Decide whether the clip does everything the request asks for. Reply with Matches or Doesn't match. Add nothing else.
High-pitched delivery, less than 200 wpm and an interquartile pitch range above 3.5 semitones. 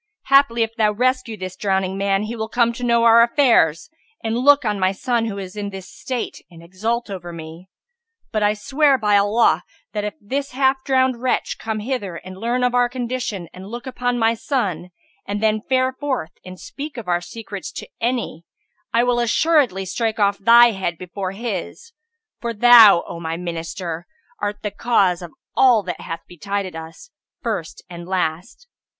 Matches